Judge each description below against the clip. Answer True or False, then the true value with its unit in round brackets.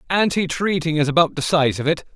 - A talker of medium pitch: True (160 Hz)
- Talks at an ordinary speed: True (195 wpm)